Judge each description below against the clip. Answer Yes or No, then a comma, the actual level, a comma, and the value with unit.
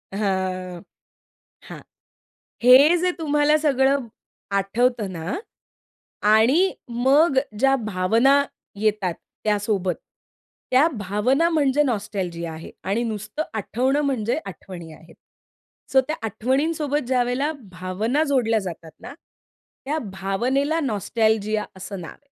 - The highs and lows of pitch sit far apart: Yes, wide, 6.0 semitones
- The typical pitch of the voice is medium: No, high, 230 Hz